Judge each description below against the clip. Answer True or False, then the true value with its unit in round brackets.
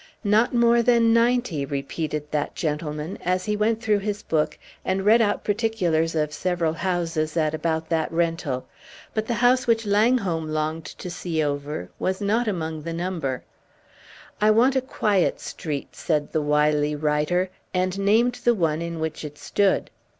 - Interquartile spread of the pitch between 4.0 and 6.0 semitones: True (5.5 semitones)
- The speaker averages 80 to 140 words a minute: False (165 wpm)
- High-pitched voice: False (175 Hz)